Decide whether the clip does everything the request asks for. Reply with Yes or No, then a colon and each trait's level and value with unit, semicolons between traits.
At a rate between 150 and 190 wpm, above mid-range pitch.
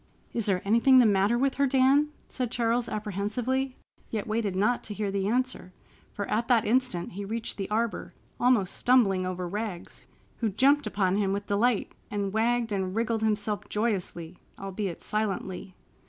Yes: average, 160 wpm; high, 215 Hz